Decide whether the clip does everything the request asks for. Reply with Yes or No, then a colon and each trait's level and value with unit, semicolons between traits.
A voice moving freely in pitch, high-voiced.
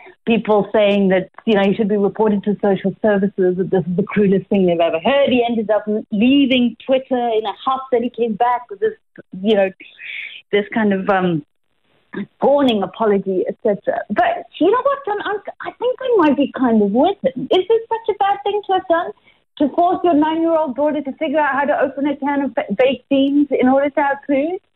Yes: wide, 7.1 semitones; very high, 260 Hz